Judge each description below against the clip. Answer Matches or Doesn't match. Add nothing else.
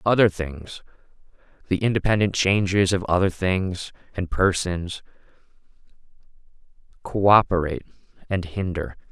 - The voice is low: Matches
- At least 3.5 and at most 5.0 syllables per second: Matches